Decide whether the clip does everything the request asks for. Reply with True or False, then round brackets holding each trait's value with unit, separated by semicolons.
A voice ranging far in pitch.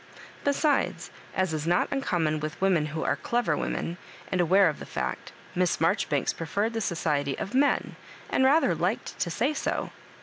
True (6.3 semitones)